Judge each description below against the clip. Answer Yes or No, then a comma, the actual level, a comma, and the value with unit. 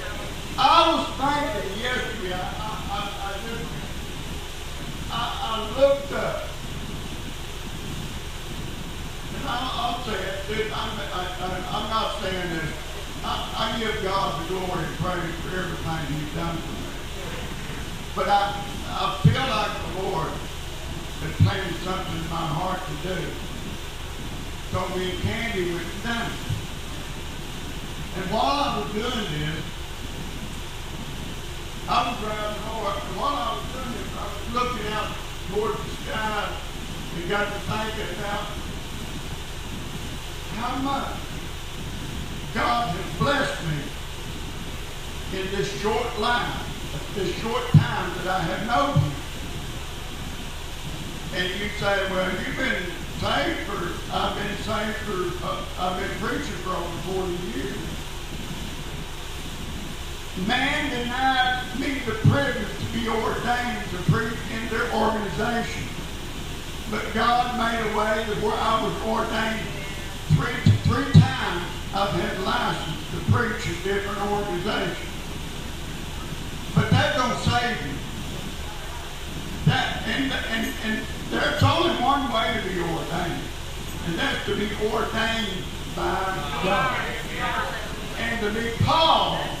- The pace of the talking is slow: Yes, slow, 125 wpm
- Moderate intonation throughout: Yes, average, 4.9 semitones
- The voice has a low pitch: No, high, 200 Hz